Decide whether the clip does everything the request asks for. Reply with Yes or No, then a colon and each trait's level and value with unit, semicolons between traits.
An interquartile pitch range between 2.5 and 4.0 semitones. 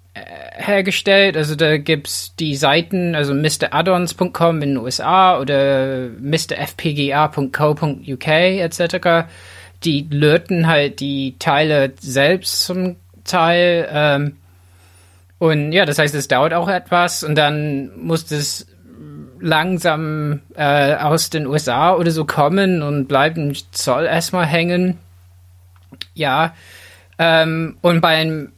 Yes: average, 3.7 semitones